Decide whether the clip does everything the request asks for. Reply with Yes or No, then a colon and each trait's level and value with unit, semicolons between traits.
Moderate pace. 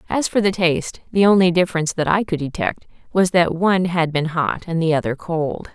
No: fast, 220 wpm